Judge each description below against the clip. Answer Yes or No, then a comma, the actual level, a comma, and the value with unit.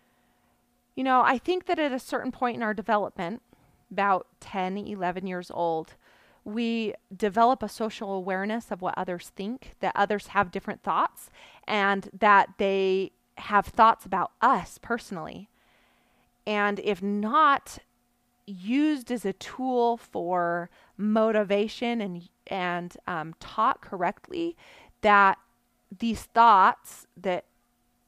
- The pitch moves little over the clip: No, average, 3.3 semitones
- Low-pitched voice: No, high, 210 Hz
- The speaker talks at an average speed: No, slow, 120 wpm